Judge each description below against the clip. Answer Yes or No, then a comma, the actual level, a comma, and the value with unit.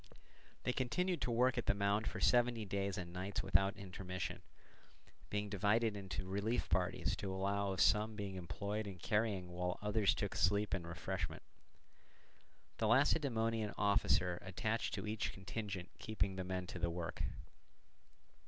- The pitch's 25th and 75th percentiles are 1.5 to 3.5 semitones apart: Yes, average, 2.8 semitones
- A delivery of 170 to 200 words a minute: No, average, 150 wpm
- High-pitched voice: No, low, 100 Hz